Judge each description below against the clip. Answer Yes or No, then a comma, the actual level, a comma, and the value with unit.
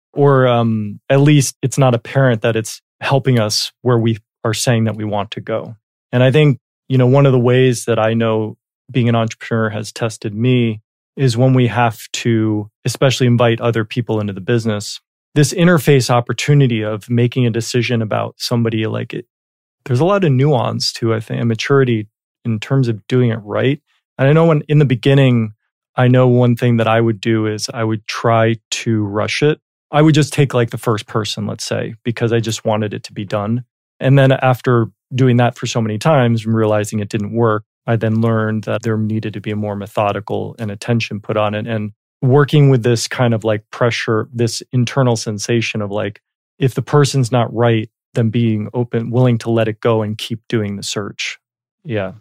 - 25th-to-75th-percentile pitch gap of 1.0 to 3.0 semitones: Yes, narrow, 2.6 semitones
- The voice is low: Yes, low, 115 Hz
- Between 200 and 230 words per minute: Yes, fast, 205 wpm